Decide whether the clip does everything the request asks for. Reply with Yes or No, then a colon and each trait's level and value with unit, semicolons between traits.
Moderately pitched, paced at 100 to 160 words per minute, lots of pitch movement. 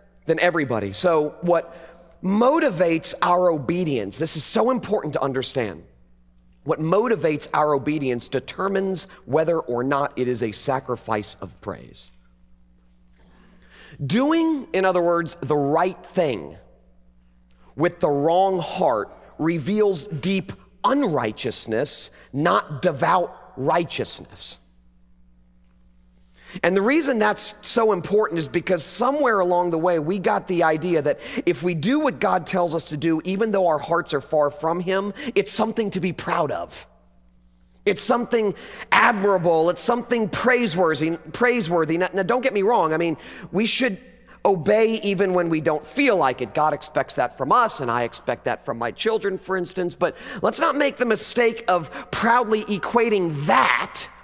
Yes: medium, 170 Hz; average, 145 wpm; wide, 6.6 semitones